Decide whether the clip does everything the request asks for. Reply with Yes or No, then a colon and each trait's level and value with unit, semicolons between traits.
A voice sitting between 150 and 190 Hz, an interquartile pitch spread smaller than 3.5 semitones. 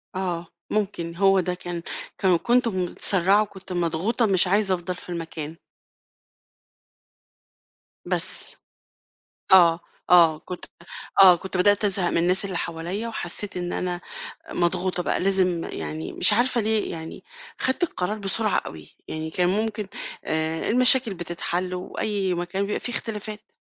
Yes: medium, 185 Hz; average, 3.1 semitones